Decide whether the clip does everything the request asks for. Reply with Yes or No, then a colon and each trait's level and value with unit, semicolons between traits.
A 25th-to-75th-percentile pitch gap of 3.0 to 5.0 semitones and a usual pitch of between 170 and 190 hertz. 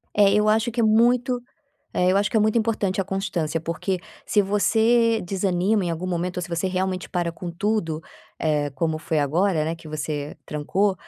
Yes: average, 4.2 semitones; medium, 185 Hz